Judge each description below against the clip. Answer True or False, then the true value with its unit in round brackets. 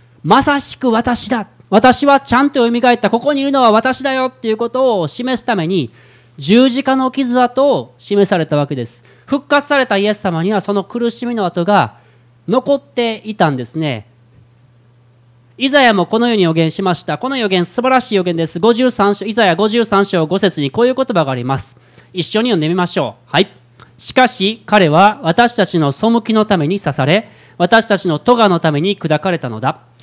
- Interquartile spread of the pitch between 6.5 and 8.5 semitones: True (7.2 semitones)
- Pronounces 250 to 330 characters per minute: False (345 characters per minute)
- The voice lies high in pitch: True (200 Hz)